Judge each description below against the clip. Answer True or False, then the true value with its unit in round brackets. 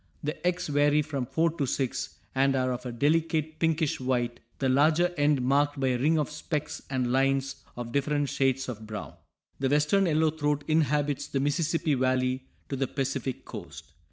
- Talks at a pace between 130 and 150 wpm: False (180 wpm)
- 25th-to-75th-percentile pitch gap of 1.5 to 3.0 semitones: True (2.6 semitones)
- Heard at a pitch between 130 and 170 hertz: True (140 Hz)